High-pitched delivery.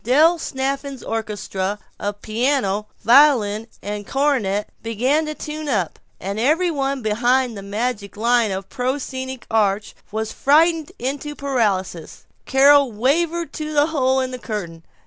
Yes: very high, 250 Hz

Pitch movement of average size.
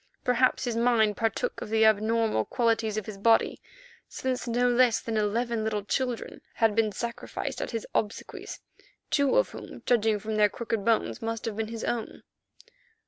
No: narrow, 1.6 semitones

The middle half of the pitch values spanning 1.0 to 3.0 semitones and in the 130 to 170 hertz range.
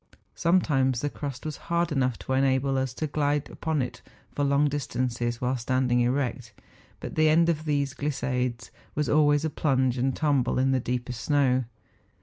Yes: average, 2.7 semitones; low, 135 Hz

